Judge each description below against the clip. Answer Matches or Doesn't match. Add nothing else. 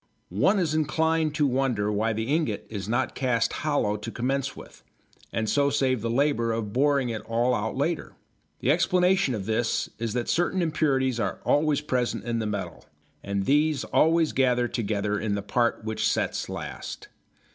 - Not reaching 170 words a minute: Doesn't match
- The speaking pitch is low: Matches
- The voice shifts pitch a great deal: Doesn't match